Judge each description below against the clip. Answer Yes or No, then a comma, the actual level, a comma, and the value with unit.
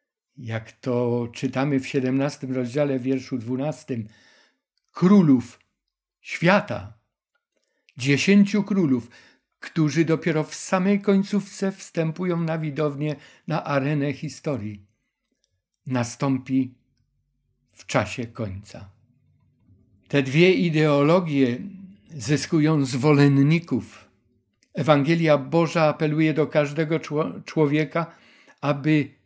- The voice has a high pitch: No, medium, 140 Hz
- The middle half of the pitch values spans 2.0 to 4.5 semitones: Yes, average, 4.2 semitones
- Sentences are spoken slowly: Yes, slow, 80 wpm